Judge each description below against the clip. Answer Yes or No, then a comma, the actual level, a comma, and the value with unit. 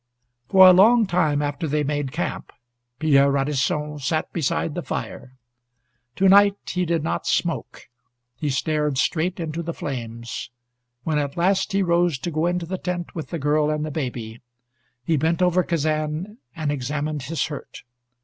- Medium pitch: Yes, medium, 155 Hz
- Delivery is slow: No, average, 165 wpm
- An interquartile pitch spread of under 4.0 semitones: Yes, average, 3.2 semitones